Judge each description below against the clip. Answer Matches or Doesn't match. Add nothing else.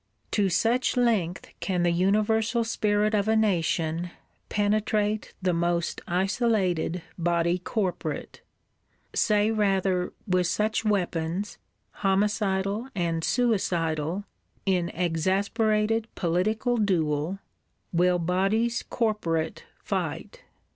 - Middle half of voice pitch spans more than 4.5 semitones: Doesn't match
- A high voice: Matches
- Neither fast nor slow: Doesn't match